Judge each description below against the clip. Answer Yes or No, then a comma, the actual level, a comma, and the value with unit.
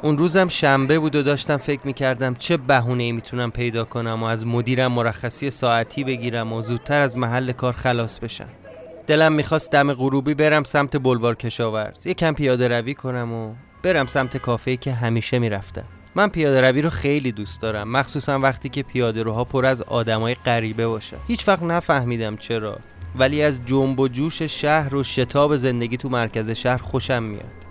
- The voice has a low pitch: Yes, low, 130 Hz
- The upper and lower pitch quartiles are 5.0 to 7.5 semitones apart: No, average, 3.6 semitones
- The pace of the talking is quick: Yes, fast, 180 wpm